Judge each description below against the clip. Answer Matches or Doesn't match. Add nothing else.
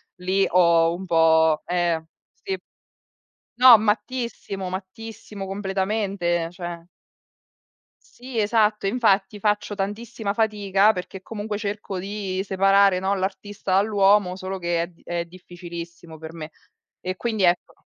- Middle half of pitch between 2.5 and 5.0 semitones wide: Matches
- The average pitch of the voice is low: Doesn't match